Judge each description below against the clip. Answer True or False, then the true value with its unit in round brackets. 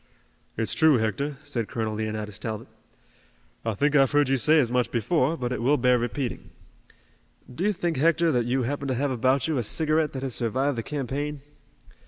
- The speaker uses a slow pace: False (195 wpm)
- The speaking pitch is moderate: False (130 Hz)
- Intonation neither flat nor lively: True (3.8 semitones)